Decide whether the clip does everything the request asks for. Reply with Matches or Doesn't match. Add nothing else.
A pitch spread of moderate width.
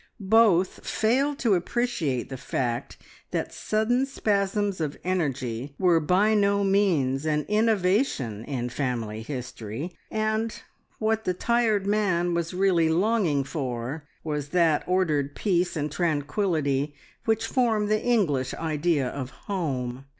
Doesn't match